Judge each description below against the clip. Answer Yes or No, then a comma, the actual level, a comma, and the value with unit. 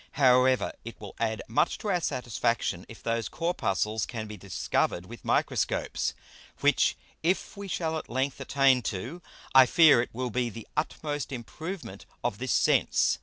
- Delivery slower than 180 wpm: Yes, average, 160 wpm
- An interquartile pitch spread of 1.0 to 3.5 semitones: No, average, 5.2 semitones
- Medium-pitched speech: No, low, 125 Hz